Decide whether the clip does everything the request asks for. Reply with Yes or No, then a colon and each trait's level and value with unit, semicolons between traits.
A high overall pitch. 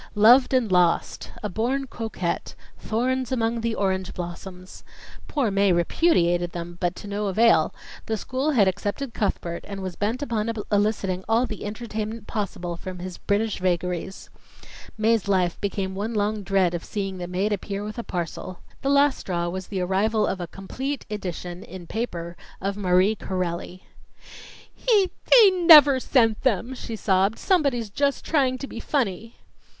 Yes: high, 205 Hz